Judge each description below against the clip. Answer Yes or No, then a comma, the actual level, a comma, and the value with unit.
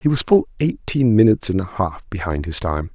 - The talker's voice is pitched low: Yes, low, 105 Hz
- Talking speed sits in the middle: No, fast, 225 wpm